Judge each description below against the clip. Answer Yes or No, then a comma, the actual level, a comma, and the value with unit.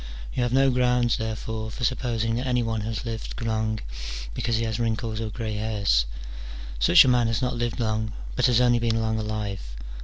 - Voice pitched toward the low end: Yes, low, 115 Hz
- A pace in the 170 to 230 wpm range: Yes, average, 195 wpm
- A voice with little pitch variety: Yes, narrow, 1.8 semitones